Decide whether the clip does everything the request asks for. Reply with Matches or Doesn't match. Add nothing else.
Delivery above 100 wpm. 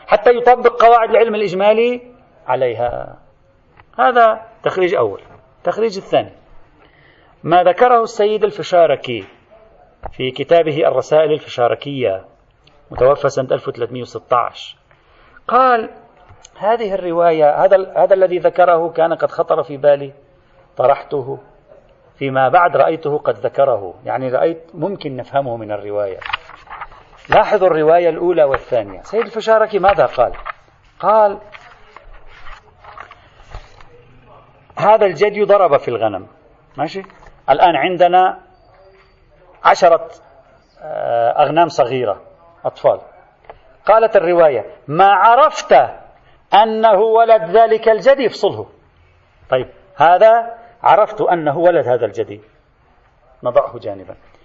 Doesn't match